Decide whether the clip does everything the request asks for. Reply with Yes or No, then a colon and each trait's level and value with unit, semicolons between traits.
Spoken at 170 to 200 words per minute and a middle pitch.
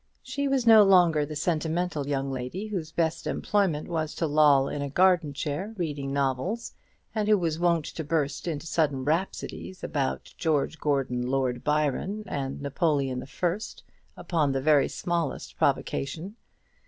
No: average, 155 wpm; medium, 155 Hz